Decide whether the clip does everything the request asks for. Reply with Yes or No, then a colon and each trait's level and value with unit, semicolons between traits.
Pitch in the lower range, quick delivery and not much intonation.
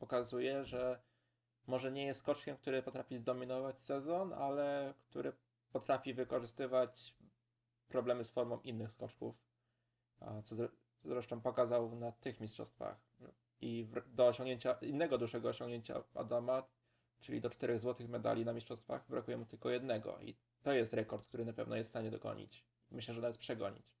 No: low, 120 Hz; average, 150 wpm; narrow, 1.6 semitones